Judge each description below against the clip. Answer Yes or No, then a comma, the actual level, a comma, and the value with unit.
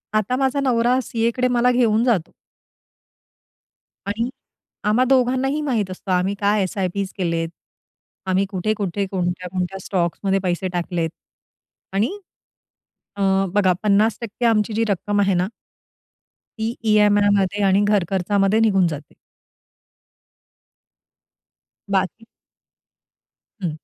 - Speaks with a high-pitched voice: Yes, high, 205 Hz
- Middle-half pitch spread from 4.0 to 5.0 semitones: No, average, 3.4 semitones